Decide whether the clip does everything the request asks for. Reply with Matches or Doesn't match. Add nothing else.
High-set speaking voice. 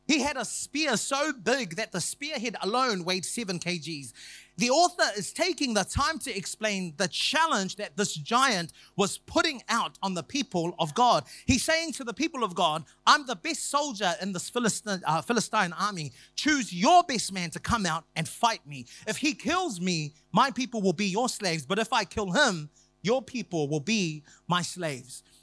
Matches